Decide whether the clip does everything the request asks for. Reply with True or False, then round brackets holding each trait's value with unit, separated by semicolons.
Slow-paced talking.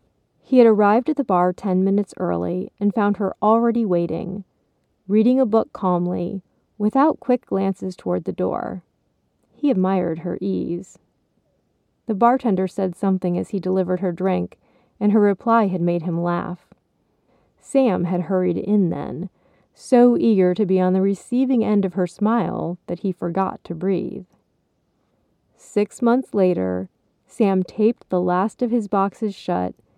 False (150 wpm)